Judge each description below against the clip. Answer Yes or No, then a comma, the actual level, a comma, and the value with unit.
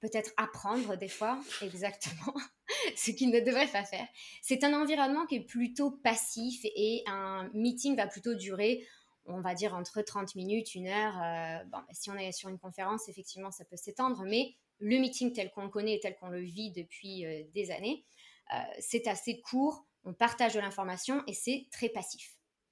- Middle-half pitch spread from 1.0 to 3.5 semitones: No, average, 4.0 semitones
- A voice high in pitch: Yes, high, 215 Hz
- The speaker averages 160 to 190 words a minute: Yes, average, 180 wpm